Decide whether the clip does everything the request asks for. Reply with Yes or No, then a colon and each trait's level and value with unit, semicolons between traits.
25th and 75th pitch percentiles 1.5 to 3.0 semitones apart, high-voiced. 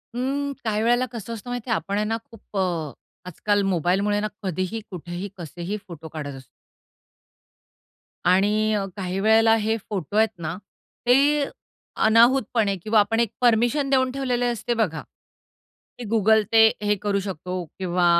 No: average, 3.8 semitones; high, 210 Hz